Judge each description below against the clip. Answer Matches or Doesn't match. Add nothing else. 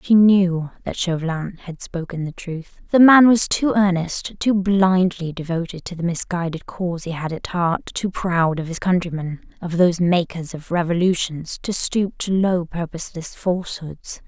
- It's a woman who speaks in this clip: Matches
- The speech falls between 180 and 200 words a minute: Doesn't match